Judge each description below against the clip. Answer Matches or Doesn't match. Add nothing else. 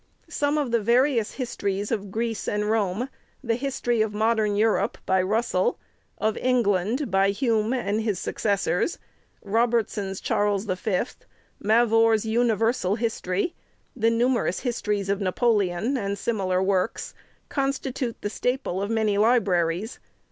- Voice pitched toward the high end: Matches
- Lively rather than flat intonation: Doesn't match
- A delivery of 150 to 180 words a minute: Doesn't match